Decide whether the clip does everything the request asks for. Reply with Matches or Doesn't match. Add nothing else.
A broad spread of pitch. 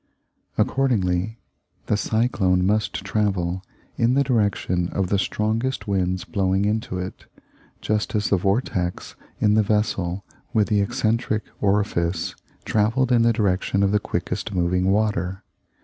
Doesn't match